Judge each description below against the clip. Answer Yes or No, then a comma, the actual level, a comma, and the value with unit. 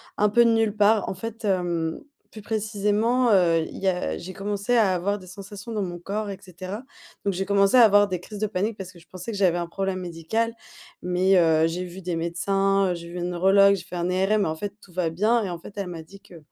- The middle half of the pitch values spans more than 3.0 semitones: No, average, 2.7 semitones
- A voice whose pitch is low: No, high, 195 Hz